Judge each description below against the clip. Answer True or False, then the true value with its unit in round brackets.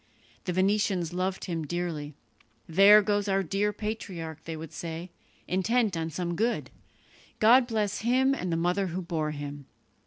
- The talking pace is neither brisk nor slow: True (155 wpm)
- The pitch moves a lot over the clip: False (4.1 semitones)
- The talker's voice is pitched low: False (185 Hz)